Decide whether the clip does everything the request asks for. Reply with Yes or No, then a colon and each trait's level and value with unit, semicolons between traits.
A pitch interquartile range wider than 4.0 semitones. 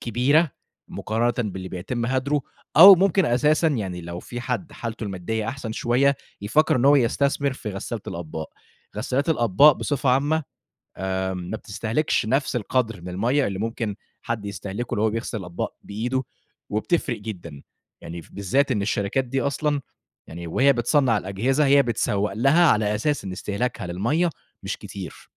Yes: wide, 5.6 semitones